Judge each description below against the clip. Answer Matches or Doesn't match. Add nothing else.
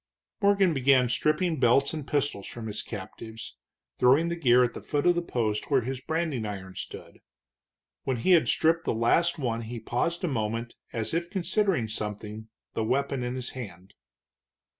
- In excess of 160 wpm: Matches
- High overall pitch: Doesn't match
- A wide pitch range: Matches